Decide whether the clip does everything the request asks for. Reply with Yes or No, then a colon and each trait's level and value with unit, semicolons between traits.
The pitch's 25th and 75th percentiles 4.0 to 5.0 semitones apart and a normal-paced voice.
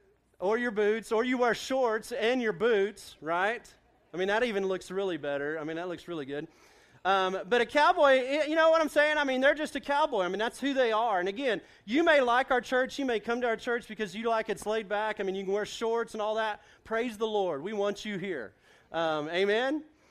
No: average, 4.7 semitones; fast, 245 wpm